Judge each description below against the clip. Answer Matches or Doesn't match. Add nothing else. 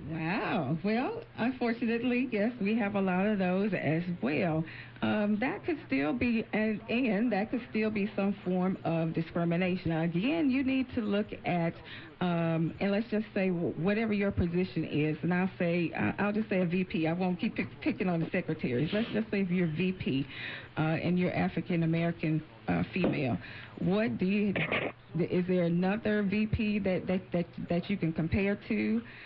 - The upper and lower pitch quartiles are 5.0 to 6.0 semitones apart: Doesn't match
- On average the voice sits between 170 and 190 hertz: Matches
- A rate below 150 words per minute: Doesn't match